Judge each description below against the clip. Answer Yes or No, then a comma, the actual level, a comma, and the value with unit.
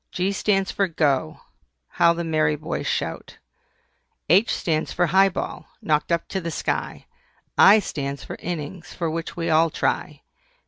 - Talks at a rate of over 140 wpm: Yes, average, 155 wpm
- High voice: No, medium, 165 Hz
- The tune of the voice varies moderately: Yes, average, 3.2 semitones